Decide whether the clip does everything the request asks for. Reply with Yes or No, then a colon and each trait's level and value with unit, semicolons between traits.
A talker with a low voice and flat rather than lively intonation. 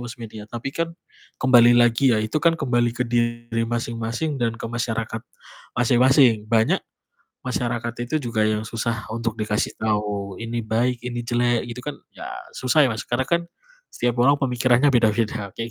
Yes: low, 120 Hz; narrow, 1.6 semitones